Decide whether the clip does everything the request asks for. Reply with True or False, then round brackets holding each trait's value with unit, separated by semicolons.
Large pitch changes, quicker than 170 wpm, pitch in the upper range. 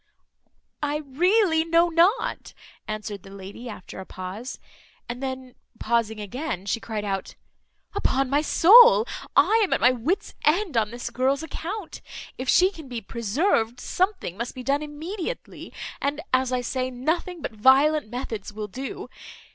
False (6.1 semitones; 155 wpm; 260 Hz)